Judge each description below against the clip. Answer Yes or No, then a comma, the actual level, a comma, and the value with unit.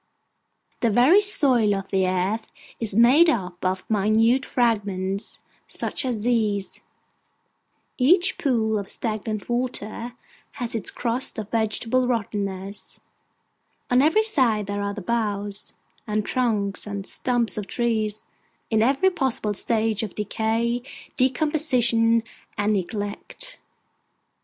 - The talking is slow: Yes, slow, 120 wpm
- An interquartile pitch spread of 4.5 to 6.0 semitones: No, average, 3.3 semitones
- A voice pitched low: No, high, 225 Hz